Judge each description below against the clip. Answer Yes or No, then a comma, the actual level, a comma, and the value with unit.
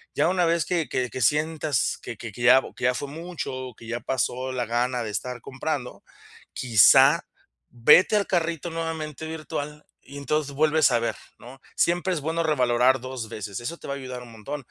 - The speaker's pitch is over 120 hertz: Yes, low, 135 Hz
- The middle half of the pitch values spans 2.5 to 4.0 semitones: No, average, 4.4 semitones